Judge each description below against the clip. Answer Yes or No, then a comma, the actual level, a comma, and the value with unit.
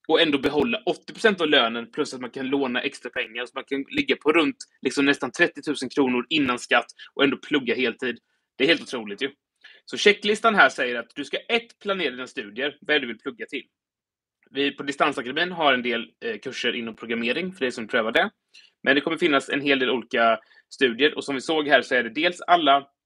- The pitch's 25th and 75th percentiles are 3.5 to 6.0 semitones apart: Yes, average, 3.8 semitones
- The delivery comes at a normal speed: No, fast, 225 wpm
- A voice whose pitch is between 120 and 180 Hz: Yes, medium, 140 Hz